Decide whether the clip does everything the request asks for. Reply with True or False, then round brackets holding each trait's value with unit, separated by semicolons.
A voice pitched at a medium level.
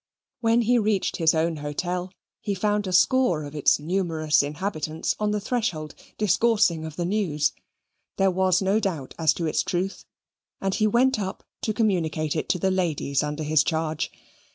True (180 Hz)